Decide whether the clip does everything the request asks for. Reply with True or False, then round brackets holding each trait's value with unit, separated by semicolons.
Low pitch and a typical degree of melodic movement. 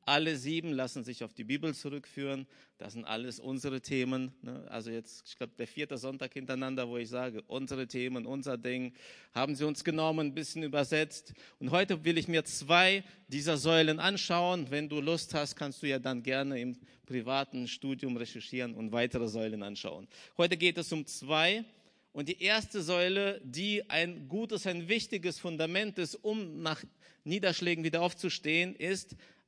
False (150 Hz; 5.0 semitones)